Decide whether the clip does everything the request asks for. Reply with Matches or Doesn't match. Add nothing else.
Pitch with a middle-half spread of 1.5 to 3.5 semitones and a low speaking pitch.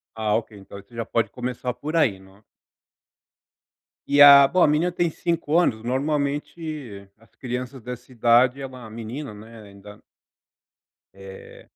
Doesn't match